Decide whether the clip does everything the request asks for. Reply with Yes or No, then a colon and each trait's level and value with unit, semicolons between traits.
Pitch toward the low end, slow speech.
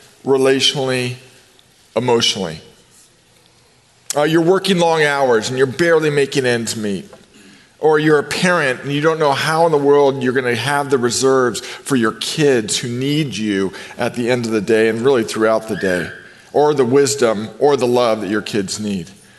No: low, 130 Hz; average, 180 wpm